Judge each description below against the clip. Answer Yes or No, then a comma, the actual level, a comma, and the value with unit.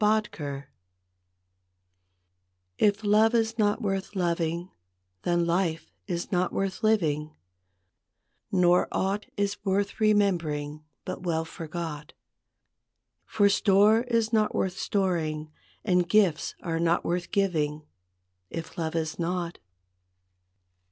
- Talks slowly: Yes, slow, 105 wpm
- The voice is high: No, medium, 180 Hz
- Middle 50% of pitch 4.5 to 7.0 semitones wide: No, average, 3.8 semitones